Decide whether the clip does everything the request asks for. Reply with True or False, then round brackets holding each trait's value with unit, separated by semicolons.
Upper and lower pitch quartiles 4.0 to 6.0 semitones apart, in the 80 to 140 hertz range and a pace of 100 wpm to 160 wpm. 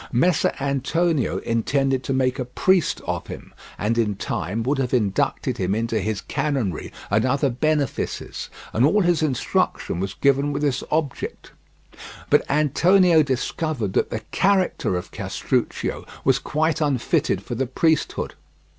True (4.9 semitones; 135 Hz; 145 wpm)